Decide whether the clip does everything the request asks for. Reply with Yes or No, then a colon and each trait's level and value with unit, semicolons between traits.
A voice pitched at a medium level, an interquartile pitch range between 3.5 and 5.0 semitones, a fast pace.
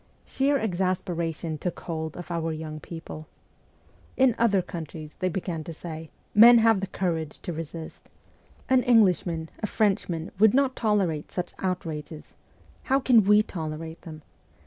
No: medium, 175 Hz; average, 4.7 semitones; average, 150 wpm